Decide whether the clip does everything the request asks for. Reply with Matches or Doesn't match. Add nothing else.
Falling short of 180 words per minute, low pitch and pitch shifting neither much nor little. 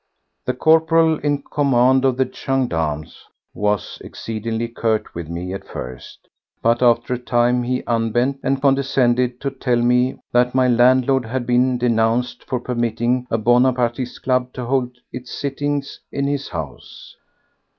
Doesn't match